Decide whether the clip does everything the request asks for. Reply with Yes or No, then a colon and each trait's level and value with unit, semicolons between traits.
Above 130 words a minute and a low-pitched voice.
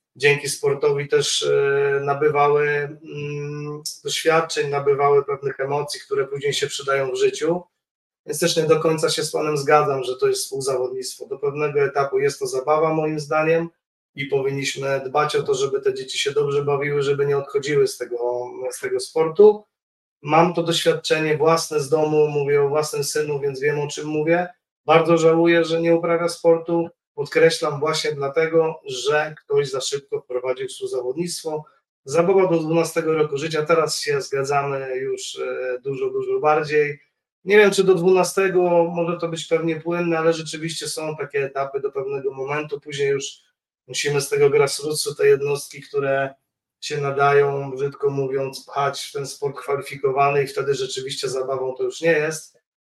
No: fast, 160 wpm; medium, 160 Hz